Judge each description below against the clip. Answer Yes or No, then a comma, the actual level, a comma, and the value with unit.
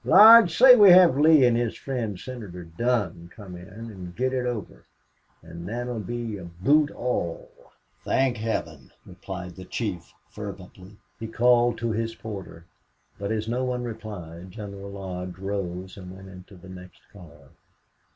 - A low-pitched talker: Yes, low, 105 Hz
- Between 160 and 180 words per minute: No, average, 150 wpm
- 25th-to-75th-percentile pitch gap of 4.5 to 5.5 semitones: Yes, average, 4.9 semitones